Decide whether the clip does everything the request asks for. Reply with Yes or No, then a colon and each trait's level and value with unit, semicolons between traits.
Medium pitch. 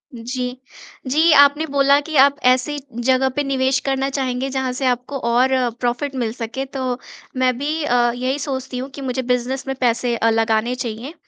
No: very high, 260 Hz